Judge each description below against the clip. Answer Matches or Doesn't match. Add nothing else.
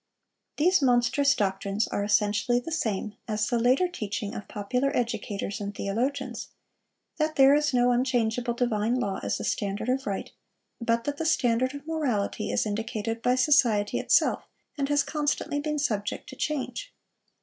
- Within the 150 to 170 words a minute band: Matches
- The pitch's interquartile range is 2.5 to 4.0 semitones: Doesn't match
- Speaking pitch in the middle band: Doesn't match